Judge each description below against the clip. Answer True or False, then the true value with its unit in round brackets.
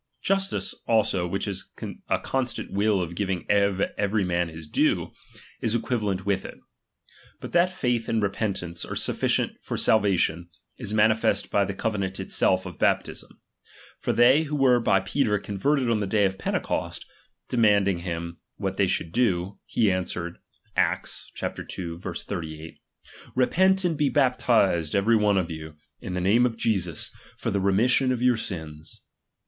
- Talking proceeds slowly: False (155 wpm)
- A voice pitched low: True (100 Hz)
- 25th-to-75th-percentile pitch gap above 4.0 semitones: True (4.5 semitones)